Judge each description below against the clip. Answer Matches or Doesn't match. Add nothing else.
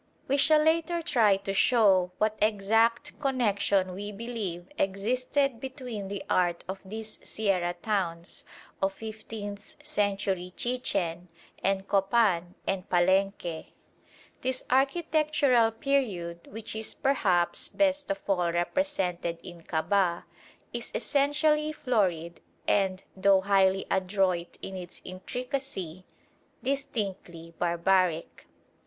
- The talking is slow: Matches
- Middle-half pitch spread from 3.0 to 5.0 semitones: Doesn't match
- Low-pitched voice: Doesn't match